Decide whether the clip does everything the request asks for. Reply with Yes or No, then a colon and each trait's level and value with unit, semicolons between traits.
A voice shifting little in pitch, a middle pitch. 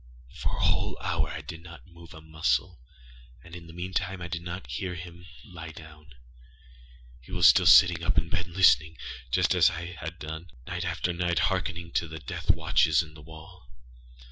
No: narrow, 1.8 semitones; very low, 85 Hz